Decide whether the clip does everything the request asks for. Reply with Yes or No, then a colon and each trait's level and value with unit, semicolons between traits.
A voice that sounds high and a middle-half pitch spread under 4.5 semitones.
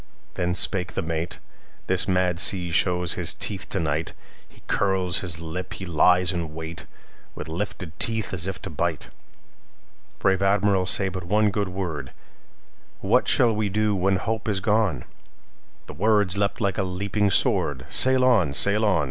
No: very low, 95 Hz; average, 2.9 semitones